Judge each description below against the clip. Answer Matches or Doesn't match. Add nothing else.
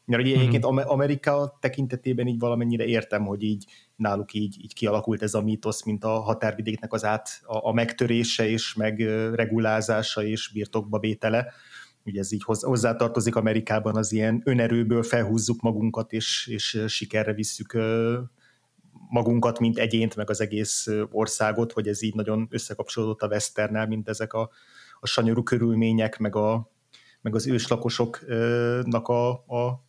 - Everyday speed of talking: Matches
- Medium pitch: Doesn't match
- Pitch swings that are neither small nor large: Doesn't match